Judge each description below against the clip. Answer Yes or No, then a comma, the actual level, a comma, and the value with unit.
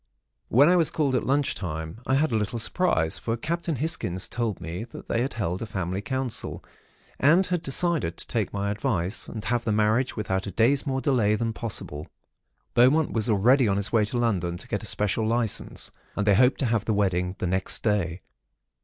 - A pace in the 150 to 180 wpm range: No, fast, 205 wpm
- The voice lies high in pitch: No, low, 110 Hz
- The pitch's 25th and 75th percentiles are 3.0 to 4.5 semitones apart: No, average, 5.1 semitones